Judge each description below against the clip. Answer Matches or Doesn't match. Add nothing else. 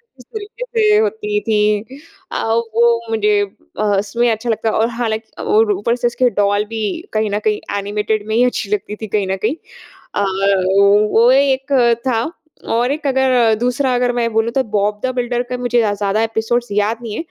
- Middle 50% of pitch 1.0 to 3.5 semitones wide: Matches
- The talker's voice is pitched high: Matches